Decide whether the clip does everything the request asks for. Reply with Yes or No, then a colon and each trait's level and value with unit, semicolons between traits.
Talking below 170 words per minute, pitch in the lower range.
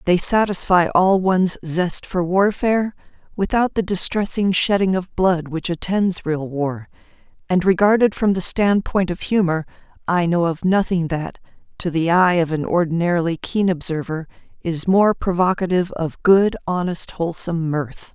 No: average, 150 wpm; medium, 180 Hz